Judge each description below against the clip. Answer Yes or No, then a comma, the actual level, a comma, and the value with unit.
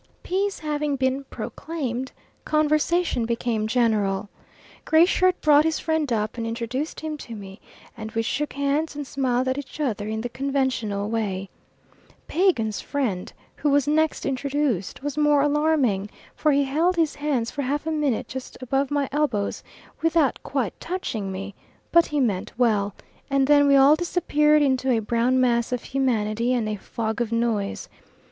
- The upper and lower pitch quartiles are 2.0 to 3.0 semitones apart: No, average, 4.7 semitones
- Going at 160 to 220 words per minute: Yes, average, 165 wpm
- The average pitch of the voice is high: Yes, very high, 265 Hz